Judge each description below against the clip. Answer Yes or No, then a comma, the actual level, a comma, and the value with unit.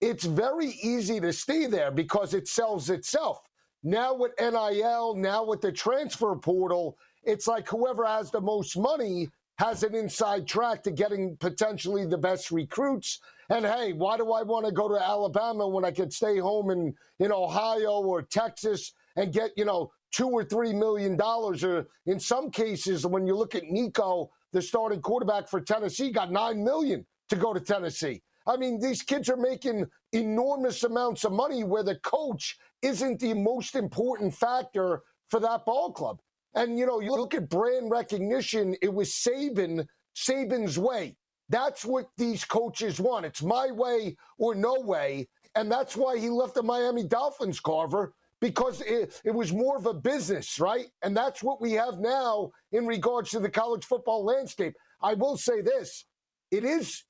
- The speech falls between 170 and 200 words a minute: Yes, average, 175 wpm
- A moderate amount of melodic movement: Yes, average, 3.8 semitones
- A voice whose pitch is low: No, high, 220 Hz